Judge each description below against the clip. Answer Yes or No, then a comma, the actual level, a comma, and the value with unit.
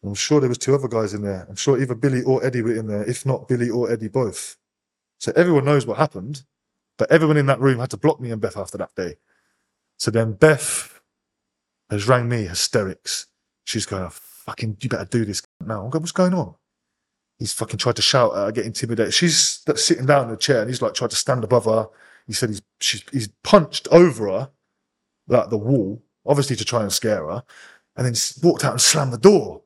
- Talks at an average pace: No, fast, 225 wpm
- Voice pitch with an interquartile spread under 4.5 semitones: No, average, 4.8 semitones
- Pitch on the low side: Yes, low, 120 Hz